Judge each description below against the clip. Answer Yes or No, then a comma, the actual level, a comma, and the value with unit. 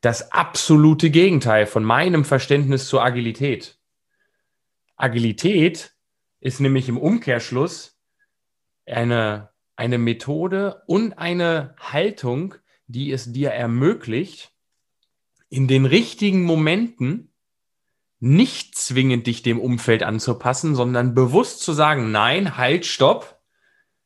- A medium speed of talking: No, slow, 100 wpm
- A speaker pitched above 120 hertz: Yes, low, 135 Hz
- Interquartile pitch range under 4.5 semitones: No, wide, 5.5 semitones